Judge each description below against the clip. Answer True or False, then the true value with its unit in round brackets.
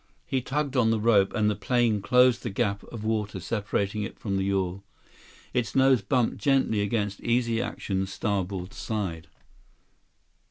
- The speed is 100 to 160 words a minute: True (155 wpm)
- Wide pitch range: False (3.5 semitones)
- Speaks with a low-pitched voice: True (105 Hz)